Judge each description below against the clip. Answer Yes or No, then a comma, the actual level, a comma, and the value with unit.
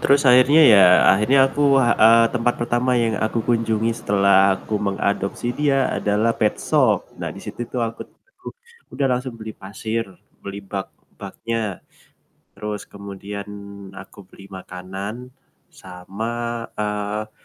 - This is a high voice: No, low, 110 Hz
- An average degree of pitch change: Yes, average, 3.0 semitones